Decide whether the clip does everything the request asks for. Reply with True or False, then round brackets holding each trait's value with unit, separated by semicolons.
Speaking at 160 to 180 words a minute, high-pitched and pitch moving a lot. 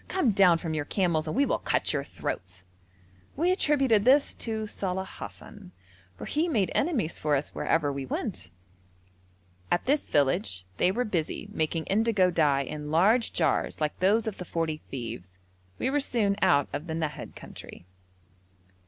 False (165 wpm; 180 Hz; 6.7 semitones)